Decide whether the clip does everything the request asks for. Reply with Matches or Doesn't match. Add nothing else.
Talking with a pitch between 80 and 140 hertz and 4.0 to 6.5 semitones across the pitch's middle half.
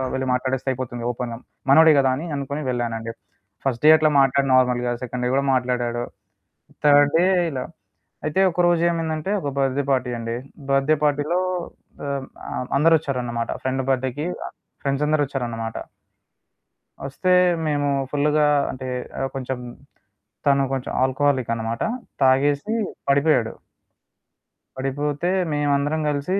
Doesn't match